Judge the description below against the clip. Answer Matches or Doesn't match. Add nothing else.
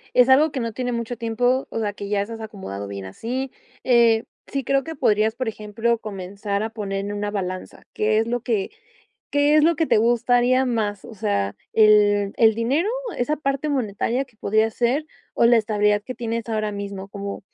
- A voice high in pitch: Matches